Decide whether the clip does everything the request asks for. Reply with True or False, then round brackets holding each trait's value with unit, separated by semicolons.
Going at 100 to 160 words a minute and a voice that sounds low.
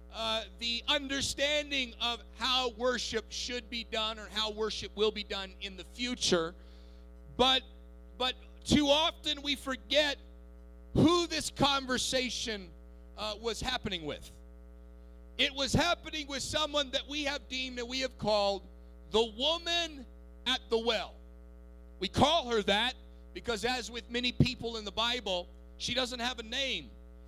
False (145 wpm; 225 Hz)